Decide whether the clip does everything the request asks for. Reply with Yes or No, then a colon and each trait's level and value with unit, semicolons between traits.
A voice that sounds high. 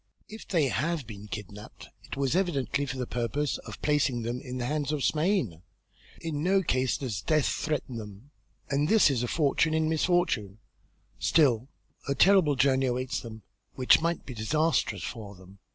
No: low, 135 Hz